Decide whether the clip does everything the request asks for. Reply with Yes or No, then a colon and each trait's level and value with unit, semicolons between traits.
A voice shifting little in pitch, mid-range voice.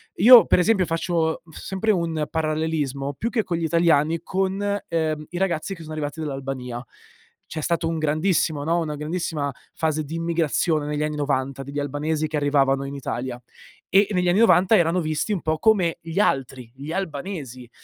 No: average, 3.4 semitones; medium, 160 Hz